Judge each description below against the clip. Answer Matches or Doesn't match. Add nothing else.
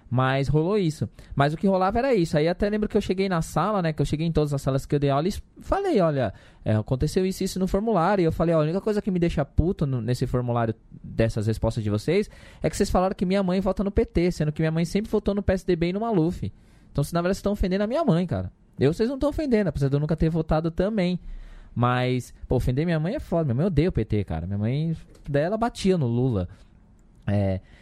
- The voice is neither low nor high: Matches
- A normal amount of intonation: Doesn't match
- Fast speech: Matches